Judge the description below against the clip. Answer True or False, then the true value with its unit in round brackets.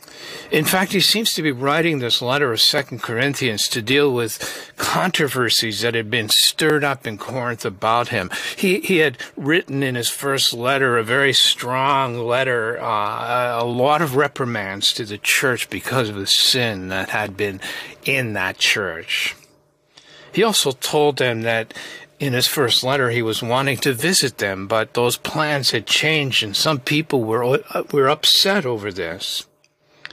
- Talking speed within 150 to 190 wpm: True (165 wpm)